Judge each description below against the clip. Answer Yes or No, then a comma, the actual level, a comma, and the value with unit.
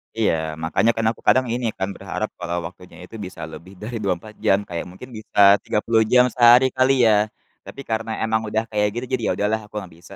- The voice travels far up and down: No, average, 3.5 semitones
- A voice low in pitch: Yes, low, 110 Hz